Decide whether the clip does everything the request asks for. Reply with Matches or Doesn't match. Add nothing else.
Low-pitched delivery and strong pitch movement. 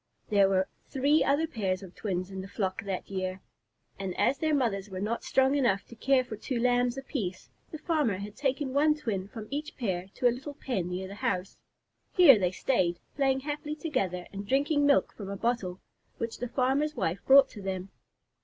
Doesn't match